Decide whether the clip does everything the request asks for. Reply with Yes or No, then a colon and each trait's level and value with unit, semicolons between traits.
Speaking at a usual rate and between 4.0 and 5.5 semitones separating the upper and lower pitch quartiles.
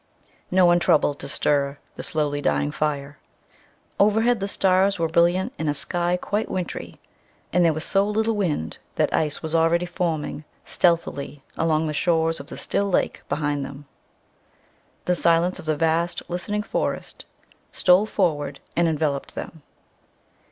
No: average, 150 wpm; average, 3.5 semitones